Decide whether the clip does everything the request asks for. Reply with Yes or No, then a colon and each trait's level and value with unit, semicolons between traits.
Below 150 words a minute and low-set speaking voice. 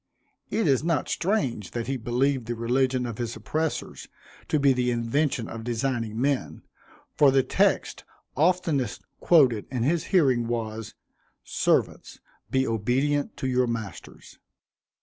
Yes: slow, 135 wpm; low, 130 Hz